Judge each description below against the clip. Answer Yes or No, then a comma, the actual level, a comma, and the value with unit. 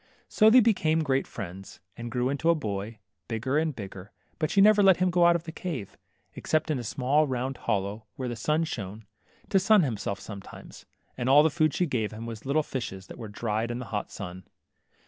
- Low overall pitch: Yes, low, 130 Hz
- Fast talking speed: Yes, fast, 220 wpm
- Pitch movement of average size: No, wide, 6.7 semitones